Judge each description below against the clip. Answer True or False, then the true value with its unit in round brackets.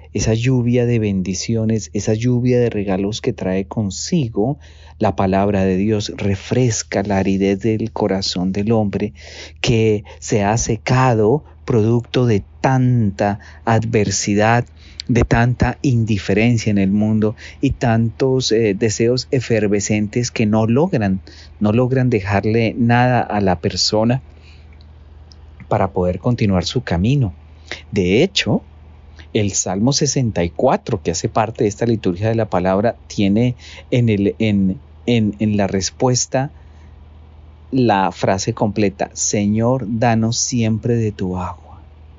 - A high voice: False (105 Hz)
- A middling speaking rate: False (125 wpm)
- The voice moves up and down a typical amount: True (4.0 semitones)